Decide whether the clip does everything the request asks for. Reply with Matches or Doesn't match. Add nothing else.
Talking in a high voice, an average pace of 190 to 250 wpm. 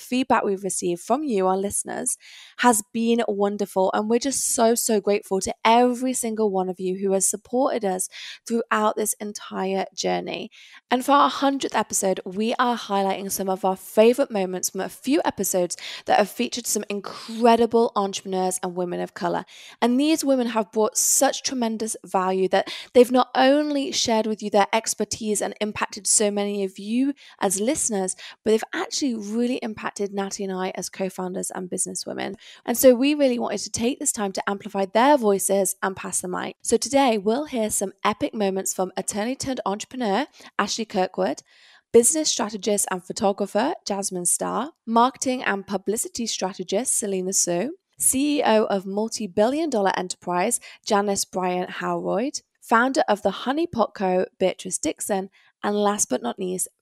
Doesn't match